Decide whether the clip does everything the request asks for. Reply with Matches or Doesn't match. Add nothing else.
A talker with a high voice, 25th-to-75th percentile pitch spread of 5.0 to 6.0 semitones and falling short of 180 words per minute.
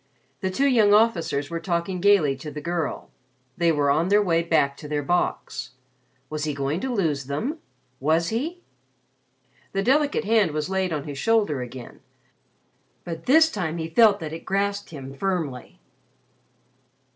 Doesn't match